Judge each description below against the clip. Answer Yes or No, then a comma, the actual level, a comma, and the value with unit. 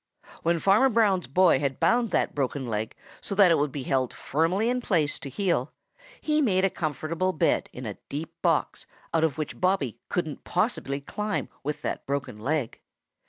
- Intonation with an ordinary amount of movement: No, wide, 5.8 semitones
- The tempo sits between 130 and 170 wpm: No, average, 180 wpm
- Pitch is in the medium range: Yes, medium, 160 Hz